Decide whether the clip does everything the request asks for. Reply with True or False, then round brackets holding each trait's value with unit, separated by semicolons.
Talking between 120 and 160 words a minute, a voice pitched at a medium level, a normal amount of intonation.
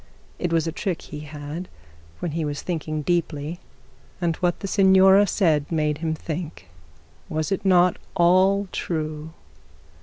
True (145 wpm; 165 Hz; 3.0 semitones)